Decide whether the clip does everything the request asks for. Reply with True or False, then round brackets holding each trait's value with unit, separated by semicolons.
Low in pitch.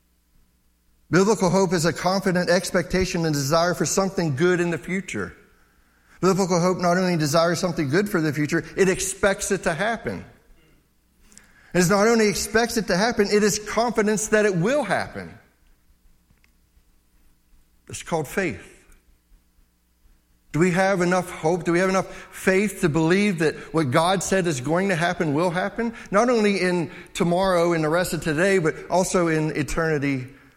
False (175 Hz)